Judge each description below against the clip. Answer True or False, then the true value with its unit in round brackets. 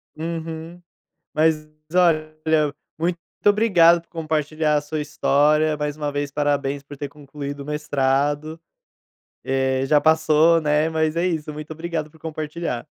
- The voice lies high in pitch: False (155 Hz)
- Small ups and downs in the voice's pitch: True (1.8 semitones)